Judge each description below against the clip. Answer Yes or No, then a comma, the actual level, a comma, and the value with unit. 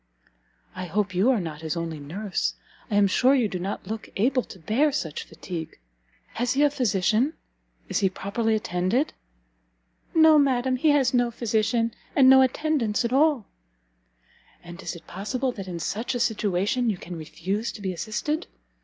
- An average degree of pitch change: No, wide, 5.7 semitones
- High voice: Yes, high, 220 Hz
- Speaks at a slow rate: No, average, 170 wpm